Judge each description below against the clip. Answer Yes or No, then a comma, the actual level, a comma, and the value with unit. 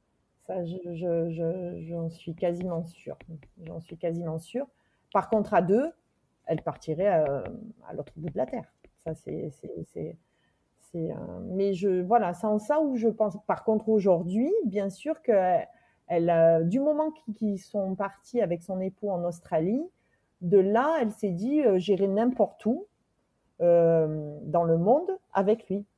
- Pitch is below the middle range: No, high, 195 Hz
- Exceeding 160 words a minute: Yes, average, 170 wpm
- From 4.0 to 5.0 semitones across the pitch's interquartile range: Yes, average, 4.5 semitones